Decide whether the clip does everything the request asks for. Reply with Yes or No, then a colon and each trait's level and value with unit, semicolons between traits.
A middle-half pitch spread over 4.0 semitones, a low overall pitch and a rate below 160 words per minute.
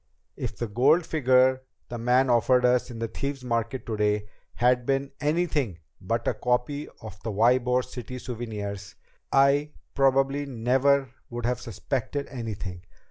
No: average, 2.9 semitones; low, 125 Hz; average, 140 wpm